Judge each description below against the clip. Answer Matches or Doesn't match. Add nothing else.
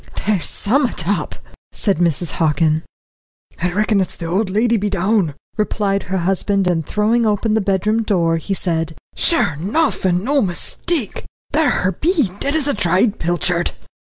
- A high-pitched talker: Matches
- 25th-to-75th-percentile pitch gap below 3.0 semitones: Doesn't match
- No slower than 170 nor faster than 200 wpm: Doesn't match